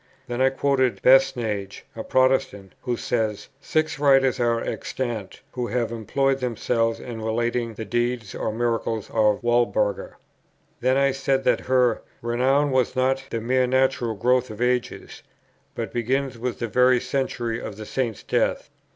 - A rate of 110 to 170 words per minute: Yes, average, 150 wpm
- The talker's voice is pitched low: Yes, low, 120 Hz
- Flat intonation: Yes, narrow, 2.3 semitones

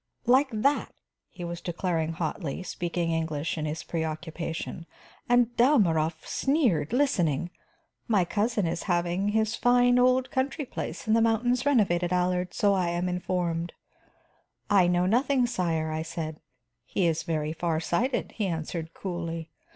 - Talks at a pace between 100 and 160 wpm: Yes, average, 145 wpm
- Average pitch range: No, wide, 5.7 semitones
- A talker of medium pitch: Yes, medium, 180 Hz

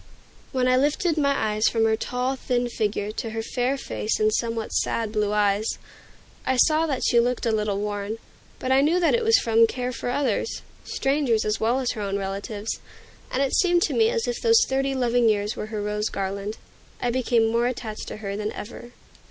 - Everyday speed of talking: No, fast, 210 wpm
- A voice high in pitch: Yes, high, 235 Hz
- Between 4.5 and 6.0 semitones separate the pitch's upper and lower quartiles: No, average, 3.8 semitones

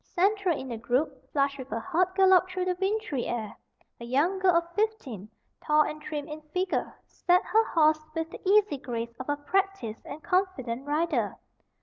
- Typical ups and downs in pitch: No, wide, 6.0 semitones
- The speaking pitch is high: Yes, very high, 310 Hz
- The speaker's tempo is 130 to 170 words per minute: No, average, 185 wpm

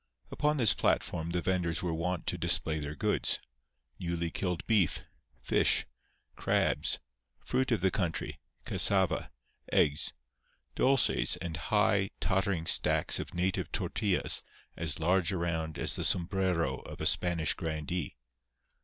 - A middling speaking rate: No, slow, 125 wpm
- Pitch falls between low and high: No, very low, 90 Hz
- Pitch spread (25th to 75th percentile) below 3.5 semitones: Yes, average, 2.9 semitones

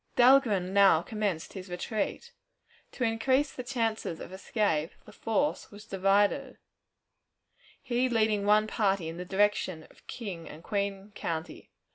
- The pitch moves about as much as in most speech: Yes, average, 3.3 semitones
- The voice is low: No, high, 205 Hz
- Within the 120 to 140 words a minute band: Yes, slow, 135 wpm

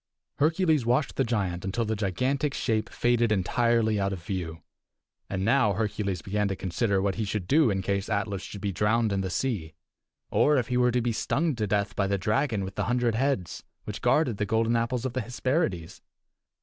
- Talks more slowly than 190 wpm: No, average, 200 wpm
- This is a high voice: No, low, 110 Hz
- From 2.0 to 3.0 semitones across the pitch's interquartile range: No, average, 4.0 semitones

